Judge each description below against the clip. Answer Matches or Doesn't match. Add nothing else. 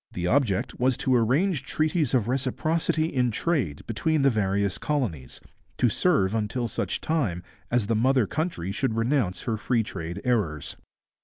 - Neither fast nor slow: Matches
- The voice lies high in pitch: Doesn't match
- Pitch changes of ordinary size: Doesn't match